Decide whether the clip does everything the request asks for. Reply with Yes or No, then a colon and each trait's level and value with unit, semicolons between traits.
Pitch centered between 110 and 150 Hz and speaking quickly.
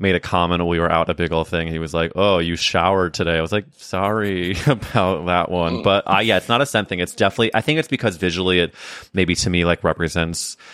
No: very low, 90 Hz; fast, 255 wpm